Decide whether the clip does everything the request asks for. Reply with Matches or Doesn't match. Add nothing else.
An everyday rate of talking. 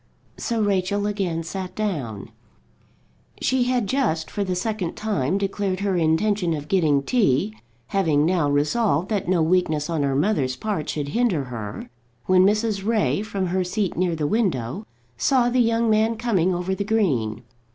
Matches